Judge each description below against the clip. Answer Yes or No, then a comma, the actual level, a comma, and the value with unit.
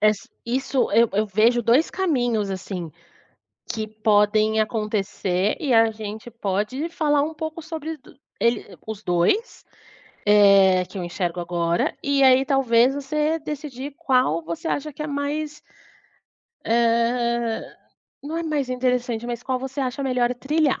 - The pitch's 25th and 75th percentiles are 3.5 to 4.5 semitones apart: No, average, 5.0 semitones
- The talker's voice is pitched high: Yes, high, 240 Hz